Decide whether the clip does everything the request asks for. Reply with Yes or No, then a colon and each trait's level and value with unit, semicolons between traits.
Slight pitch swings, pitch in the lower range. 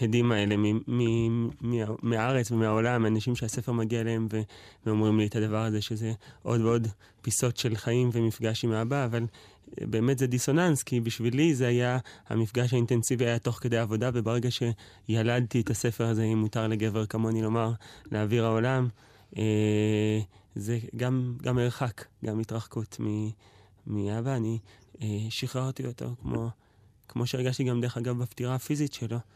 Yes: narrow, 2.0 semitones; low, 115 Hz